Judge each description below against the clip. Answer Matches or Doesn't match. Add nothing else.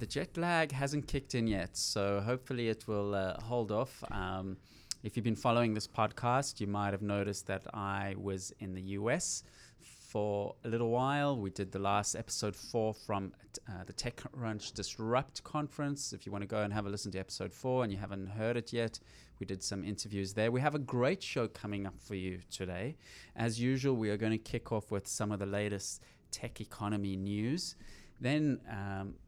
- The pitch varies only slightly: Doesn't match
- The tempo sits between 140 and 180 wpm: Doesn't match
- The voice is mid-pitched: Doesn't match